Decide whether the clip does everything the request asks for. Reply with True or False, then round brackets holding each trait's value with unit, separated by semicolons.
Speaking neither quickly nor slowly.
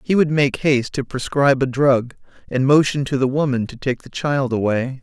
False (215 wpm)